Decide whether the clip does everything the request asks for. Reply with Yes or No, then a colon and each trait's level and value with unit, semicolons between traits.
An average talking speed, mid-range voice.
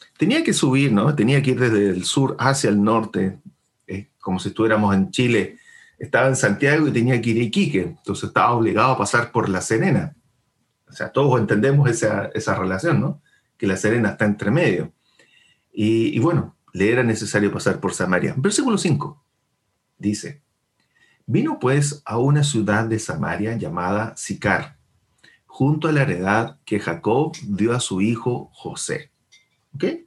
No: average, 165 wpm; low, 120 Hz